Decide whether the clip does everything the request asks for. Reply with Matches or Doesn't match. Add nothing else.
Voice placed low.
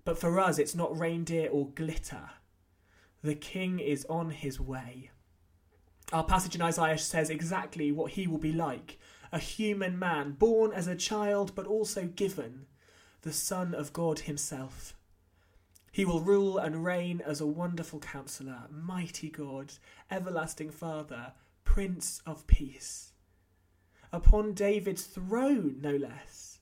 Doesn't match